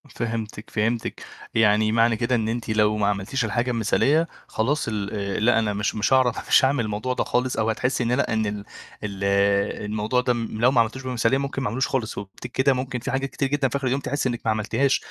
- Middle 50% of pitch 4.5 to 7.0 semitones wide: No, average, 3.4 semitones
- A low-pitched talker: Yes, low, 115 Hz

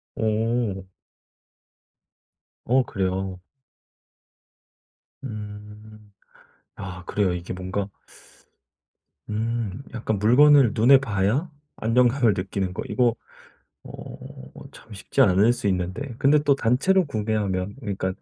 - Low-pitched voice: Yes, low, 105 Hz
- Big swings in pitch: No, average, 4.2 semitones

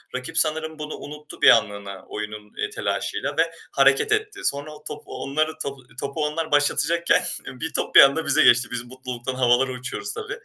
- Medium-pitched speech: Yes, medium, 145 Hz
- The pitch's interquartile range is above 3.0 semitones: Yes, average, 3.9 semitones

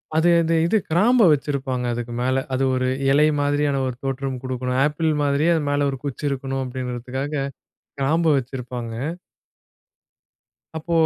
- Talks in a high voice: No, low, 135 Hz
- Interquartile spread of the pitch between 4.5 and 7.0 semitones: No, narrow, 2.6 semitones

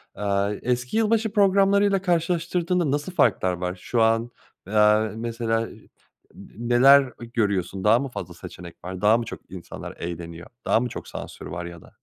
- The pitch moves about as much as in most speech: No, wide, 9.0 semitones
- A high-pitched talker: No, low, 115 Hz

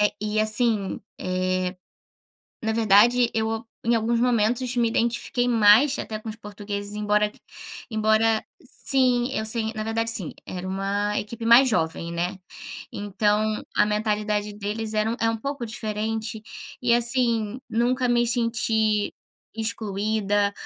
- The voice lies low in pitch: No, high, 220 Hz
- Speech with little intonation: Yes, narrow, 2.0 semitones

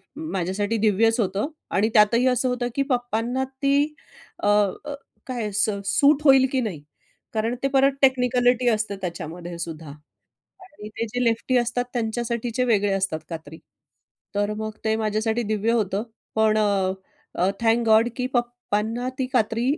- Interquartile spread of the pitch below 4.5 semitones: Yes, average, 3.2 semitones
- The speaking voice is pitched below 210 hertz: No, high, 225 Hz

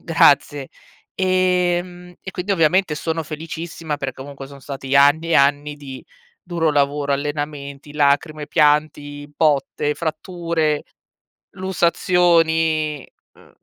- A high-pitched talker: No, medium, 155 Hz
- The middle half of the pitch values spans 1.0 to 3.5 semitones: Yes, average, 2.7 semitones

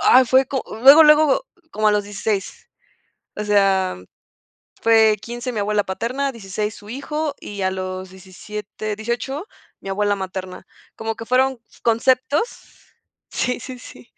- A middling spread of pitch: Yes, average, 4.3 semitones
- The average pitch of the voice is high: Yes, high, 220 Hz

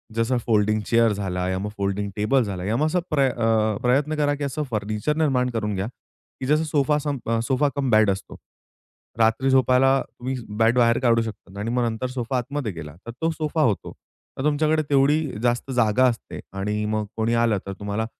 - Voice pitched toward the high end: No, low, 120 Hz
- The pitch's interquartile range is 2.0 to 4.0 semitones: No, average, 4.5 semitones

